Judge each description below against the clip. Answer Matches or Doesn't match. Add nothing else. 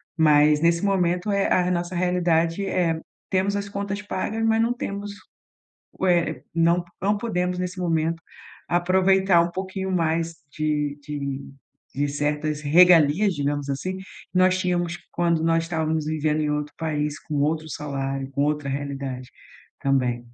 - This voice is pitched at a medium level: Matches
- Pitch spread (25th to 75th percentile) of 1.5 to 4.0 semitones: Matches